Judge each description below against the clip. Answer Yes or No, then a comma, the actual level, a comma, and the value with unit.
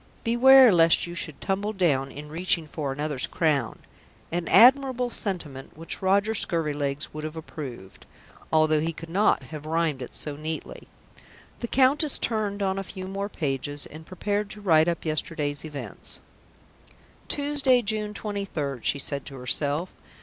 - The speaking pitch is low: No, medium, 165 Hz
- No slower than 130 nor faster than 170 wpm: Yes, average, 155 wpm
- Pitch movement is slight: No, wide, 5.6 semitones